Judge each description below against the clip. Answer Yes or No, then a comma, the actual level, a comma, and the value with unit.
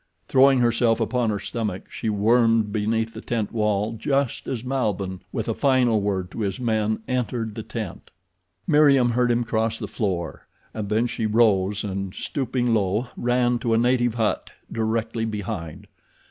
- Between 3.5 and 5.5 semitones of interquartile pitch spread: No, narrow, 2.5 semitones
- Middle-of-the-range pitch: No, low, 115 Hz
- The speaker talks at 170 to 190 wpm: No, average, 160 wpm